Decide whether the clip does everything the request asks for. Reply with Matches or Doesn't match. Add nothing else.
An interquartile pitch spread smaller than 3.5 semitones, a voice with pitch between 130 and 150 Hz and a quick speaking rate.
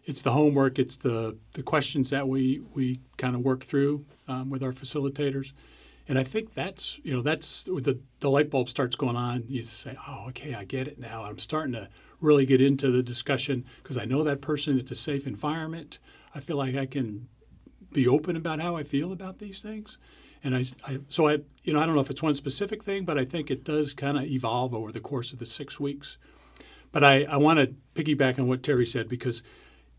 Matches